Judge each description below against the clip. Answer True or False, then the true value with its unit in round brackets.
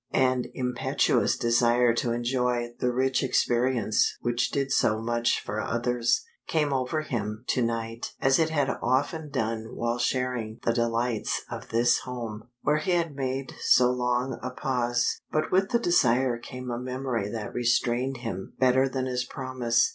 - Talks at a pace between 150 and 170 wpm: True (160 wpm)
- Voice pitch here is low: True (125 Hz)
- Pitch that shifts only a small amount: True (1.9 semitones)